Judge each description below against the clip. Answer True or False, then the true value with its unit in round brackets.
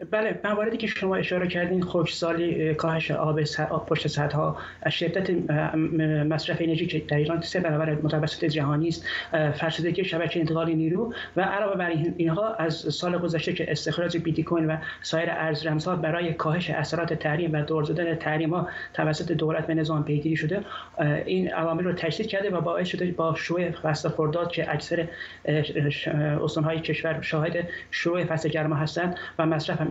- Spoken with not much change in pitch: True (1.6 semitones)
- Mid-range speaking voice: True (160 Hz)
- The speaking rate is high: True (165 wpm)